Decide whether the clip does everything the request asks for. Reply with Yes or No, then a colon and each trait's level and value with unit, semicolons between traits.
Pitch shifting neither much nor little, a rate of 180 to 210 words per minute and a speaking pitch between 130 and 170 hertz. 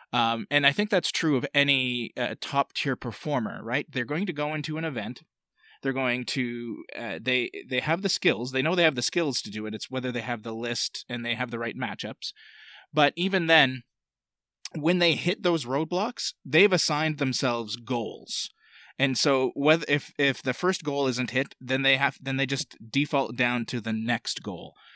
Yes: average, 4.1 semitones; average, 200 wpm; low, 135 Hz